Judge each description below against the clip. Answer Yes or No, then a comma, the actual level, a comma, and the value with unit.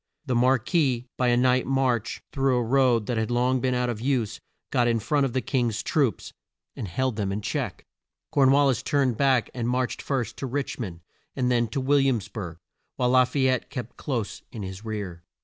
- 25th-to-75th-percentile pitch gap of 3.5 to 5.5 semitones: No, average, 2.8 semitones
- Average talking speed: No, fast, 215 wpm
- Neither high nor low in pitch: No, low, 125 Hz